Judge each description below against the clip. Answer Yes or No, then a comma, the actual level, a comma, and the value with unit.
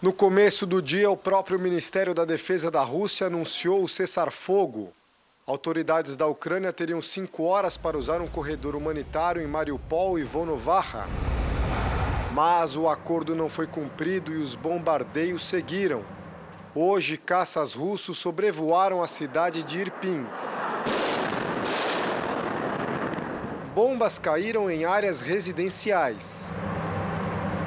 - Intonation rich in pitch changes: No, average, 2.9 semitones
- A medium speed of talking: No, slow, 115 wpm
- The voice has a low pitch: No, medium, 170 Hz